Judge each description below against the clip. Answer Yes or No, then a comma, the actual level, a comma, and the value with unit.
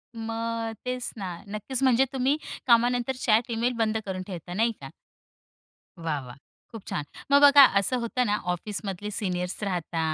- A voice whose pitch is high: Yes, high, 225 Hz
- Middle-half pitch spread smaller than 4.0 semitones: No, average, 4.8 semitones